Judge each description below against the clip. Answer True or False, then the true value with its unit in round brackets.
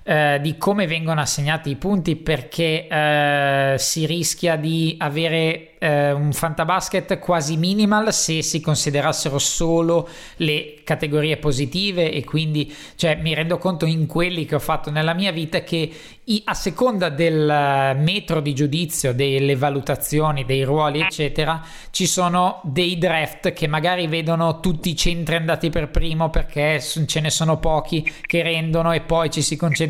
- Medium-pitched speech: True (160 Hz)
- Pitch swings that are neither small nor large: False (1.9 semitones)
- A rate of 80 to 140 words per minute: False (150 wpm)